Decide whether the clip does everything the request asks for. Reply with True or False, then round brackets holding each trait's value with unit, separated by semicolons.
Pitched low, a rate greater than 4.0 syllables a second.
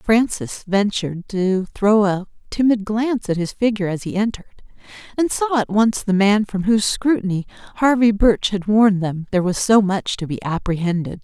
False (205 Hz; 5.3 syllables/s)